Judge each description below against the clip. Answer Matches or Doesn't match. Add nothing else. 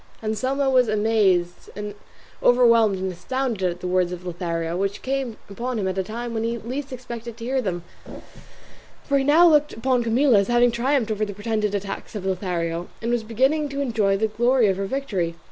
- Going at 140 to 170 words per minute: Doesn't match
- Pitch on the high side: Matches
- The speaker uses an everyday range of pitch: Matches